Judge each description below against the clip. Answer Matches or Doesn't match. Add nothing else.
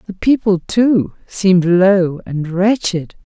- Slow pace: Matches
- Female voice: Matches